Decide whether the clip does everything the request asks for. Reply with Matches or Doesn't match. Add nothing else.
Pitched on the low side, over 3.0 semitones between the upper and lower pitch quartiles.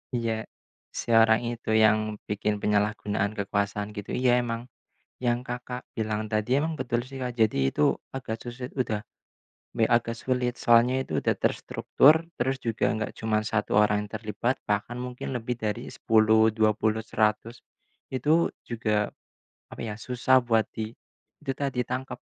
Doesn't match